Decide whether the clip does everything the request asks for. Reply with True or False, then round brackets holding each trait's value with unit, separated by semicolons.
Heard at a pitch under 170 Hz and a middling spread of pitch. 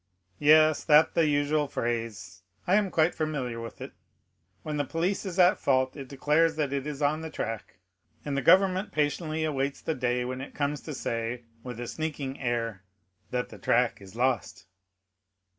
True (140 Hz; 4.2 semitones)